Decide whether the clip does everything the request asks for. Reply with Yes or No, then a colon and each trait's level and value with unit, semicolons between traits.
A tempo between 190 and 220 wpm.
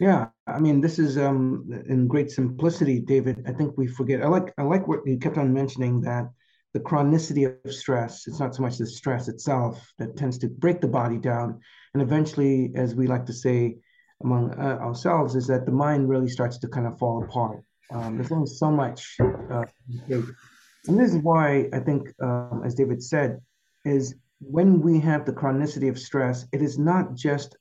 Yes: average, 200 wpm